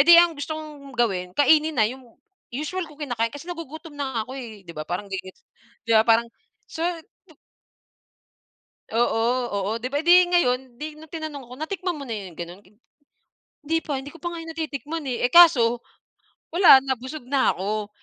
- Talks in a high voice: Yes, very high, 275 Hz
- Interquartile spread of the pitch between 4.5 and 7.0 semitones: Yes, average, 5.3 semitones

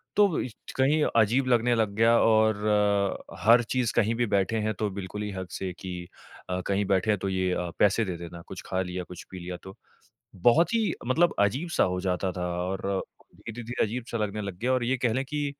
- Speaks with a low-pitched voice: Yes, low, 105 Hz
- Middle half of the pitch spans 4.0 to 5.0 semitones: Yes, average, 4.3 semitones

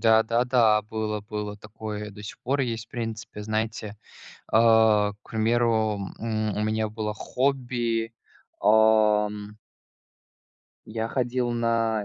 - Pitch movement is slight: Yes, narrow, 1.5 semitones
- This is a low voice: Yes, low, 110 Hz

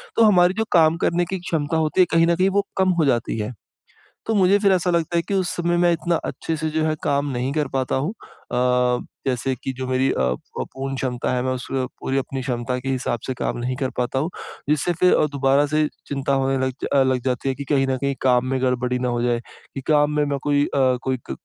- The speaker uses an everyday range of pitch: Yes, average, 4.1 semitones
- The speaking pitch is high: No, low, 135 Hz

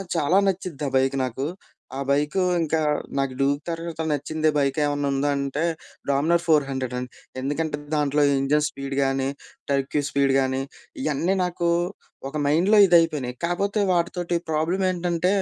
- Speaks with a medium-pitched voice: Yes, medium, 150 Hz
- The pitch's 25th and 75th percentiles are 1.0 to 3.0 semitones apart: No, average, 3.7 semitones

